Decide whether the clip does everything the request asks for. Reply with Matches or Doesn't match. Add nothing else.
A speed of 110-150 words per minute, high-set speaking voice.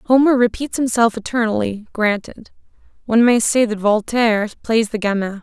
Matches